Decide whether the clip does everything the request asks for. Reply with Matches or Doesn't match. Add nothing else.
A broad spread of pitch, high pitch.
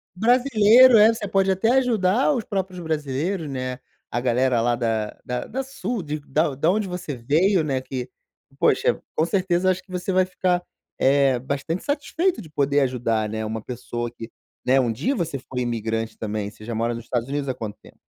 Doesn't match